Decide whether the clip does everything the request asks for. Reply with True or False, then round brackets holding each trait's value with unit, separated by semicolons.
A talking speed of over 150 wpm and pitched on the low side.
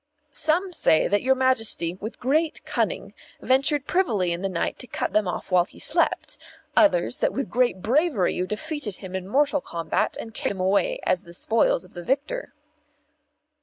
False (180 wpm; 230 Hz)